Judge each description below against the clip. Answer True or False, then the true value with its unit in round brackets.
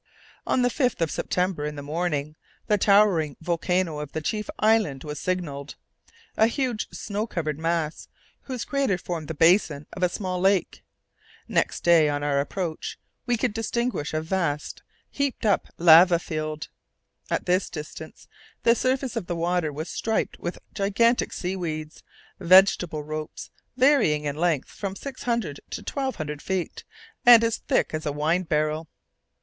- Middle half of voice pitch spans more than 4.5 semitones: True (5.5 semitones)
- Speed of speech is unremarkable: True (155 wpm)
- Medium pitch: True (175 Hz)